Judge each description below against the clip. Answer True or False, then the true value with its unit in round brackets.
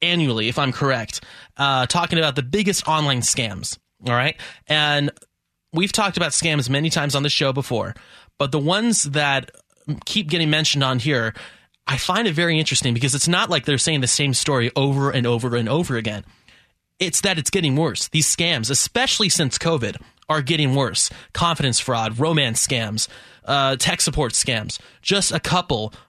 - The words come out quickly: False (175 wpm)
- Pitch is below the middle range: False (145 Hz)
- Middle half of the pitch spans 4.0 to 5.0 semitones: True (4.6 semitones)